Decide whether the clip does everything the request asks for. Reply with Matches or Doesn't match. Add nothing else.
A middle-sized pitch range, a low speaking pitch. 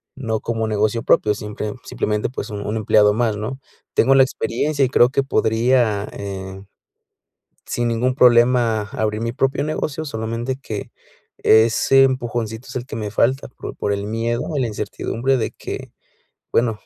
Matches